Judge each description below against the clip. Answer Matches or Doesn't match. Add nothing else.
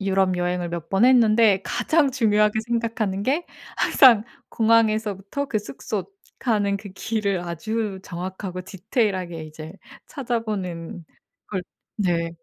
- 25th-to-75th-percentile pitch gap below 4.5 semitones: Matches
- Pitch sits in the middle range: Doesn't match